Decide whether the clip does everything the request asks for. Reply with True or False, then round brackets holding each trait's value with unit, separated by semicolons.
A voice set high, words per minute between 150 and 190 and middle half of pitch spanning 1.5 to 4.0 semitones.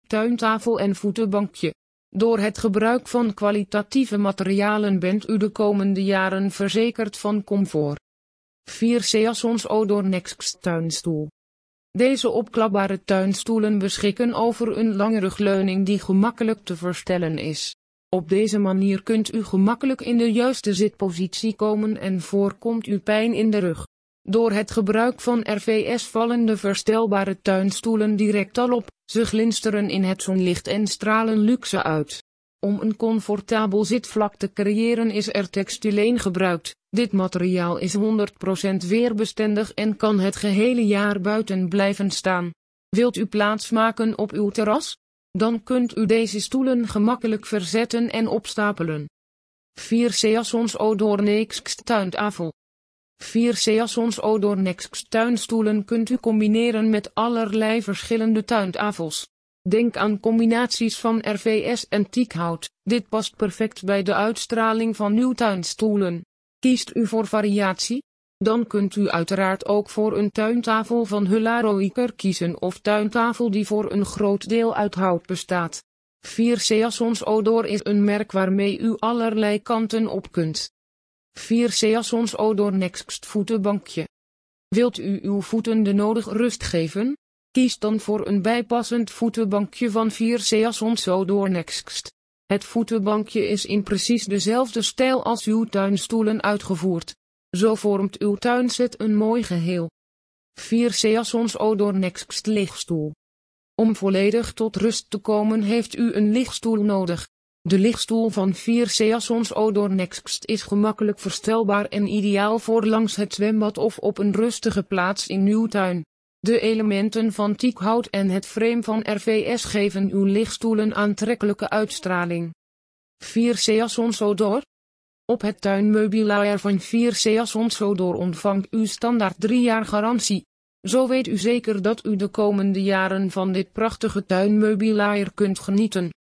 False (210 Hz; 135 wpm; 2.4 semitones)